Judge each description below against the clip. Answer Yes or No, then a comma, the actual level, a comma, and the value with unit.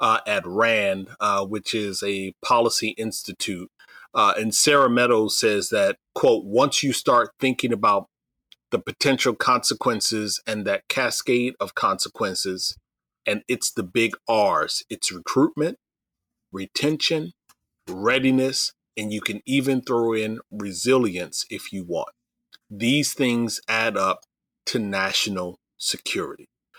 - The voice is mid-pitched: No, low, 110 Hz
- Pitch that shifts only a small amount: No, average, 4.5 semitones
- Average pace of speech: No, slow, 125 wpm